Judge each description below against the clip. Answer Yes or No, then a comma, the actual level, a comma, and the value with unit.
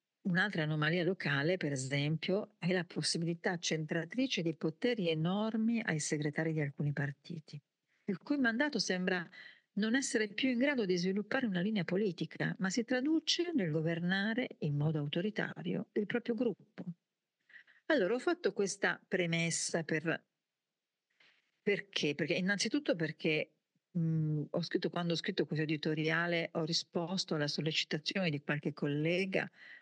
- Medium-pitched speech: Yes, medium, 175 Hz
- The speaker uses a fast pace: No, average, 135 wpm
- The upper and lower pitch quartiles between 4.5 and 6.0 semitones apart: Yes, average, 4.8 semitones